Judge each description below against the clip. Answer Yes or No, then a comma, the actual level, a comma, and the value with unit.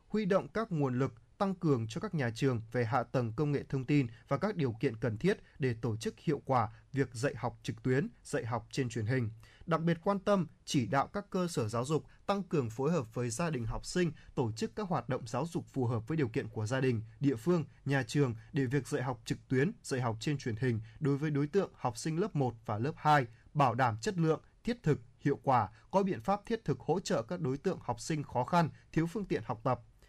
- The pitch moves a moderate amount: Yes, average, 4.8 semitones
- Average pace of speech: No, fast, 255 wpm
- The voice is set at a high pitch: No, medium, 140 Hz